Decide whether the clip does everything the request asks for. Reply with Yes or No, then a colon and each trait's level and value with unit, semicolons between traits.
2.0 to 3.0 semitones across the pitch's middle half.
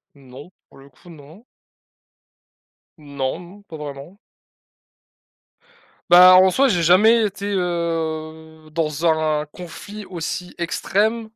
No: average, 3.5 semitones